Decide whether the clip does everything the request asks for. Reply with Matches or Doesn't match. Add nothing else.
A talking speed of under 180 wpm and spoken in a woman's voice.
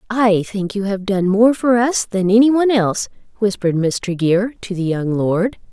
Doesn't match